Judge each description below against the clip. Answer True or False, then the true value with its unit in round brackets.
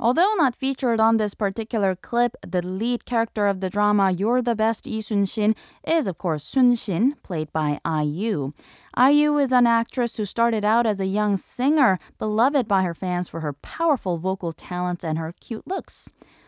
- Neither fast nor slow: True (180 wpm)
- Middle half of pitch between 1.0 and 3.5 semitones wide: False (4.6 semitones)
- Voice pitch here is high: True (215 Hz)